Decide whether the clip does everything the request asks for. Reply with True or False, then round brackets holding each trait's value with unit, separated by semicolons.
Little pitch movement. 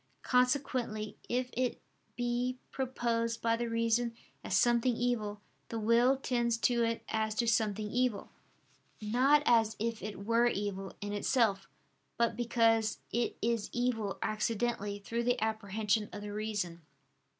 True (2.2 semitones)